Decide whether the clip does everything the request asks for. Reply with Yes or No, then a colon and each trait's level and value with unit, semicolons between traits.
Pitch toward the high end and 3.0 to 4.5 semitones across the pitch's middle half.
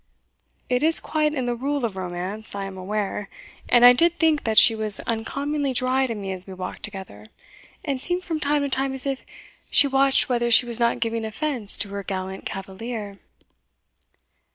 No: high, 235 Hz; wide, 5.5 semitones